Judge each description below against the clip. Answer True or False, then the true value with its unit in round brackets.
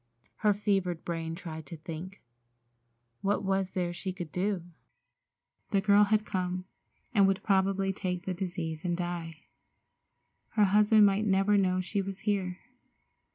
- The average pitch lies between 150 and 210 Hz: True (190 Hz)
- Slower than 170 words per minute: True (145 wpm)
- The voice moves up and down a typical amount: False (2.3 semitones)